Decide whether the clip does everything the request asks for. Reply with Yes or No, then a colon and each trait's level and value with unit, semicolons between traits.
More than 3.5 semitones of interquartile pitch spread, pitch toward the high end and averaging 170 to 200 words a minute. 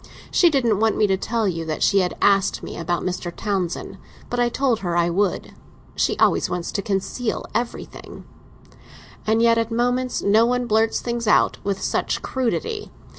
Yes: average, 4.0 semitones; high, 220 Hz; average, 175 wpm